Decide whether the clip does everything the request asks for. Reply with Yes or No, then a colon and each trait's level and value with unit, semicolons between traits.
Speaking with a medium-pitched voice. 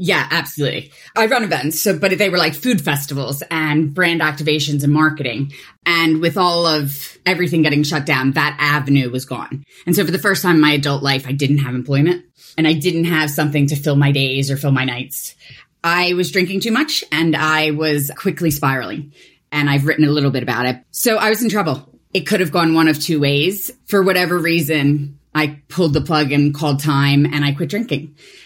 Yes: medium, 155 Hz